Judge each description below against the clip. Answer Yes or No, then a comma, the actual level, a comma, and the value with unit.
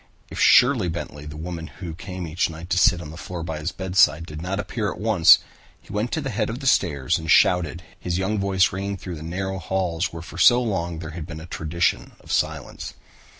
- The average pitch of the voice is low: Yes, very low, 90 Hz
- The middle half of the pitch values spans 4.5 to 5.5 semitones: No, average, 2.9 semitones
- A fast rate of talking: Yes, fast, 230 wpm